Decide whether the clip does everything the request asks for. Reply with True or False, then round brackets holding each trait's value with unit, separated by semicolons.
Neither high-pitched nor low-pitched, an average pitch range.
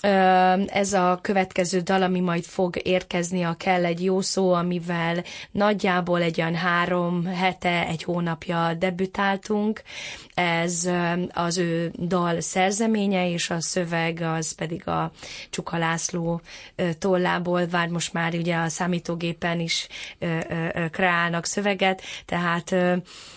False (175 Hz; 1.6 semitones)